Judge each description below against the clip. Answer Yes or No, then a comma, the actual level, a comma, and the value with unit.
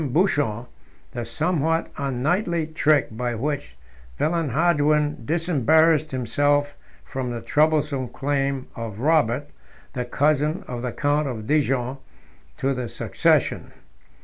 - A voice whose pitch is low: No, medium, 145 Hz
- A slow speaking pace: Yes, slow, 110 wpm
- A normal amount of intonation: Yes, average, 3.6 semitones